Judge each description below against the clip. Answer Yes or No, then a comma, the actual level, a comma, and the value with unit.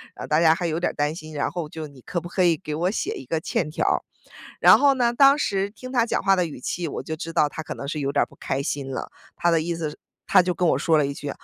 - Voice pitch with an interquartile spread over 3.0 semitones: Yes, average, 3.4 semitones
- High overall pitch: No, medium, 165 Hz